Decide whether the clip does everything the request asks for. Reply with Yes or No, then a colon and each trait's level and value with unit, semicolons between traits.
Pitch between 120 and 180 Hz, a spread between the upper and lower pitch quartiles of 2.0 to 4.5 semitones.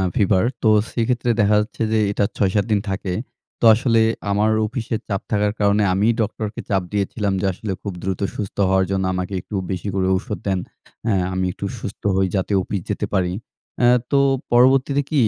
No: low, 105 Hz; narrow, 2.5 semitones